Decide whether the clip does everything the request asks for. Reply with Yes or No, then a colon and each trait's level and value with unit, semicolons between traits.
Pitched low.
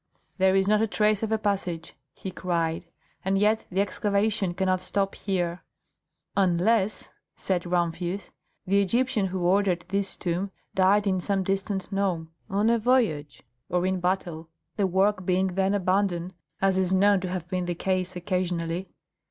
No: high, 190 Hz